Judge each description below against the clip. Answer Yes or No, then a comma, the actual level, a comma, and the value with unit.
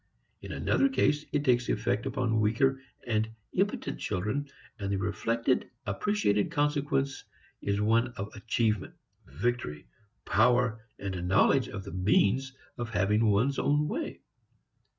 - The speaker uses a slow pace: Yes, slow, 130 wpm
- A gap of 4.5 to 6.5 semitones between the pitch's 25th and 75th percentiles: Yes, average, 4.9 semitones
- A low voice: Yes, low, 115 Hz